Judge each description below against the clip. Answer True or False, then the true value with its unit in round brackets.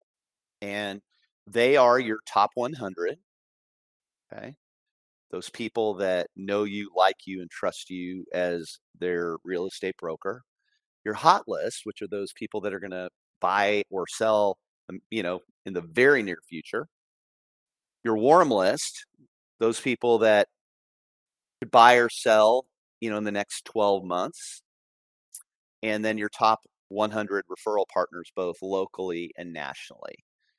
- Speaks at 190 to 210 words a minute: False (140 wpm)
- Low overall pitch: True (100 Hz)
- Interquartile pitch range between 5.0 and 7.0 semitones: False (3.3 semitones)